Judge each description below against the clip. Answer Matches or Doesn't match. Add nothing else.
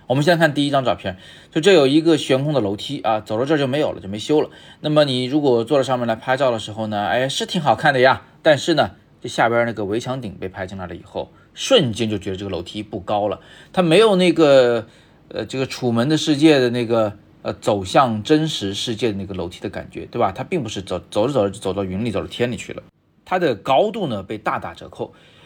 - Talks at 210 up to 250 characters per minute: Doesn't match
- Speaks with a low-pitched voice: Matches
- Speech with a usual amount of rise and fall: Doesn't match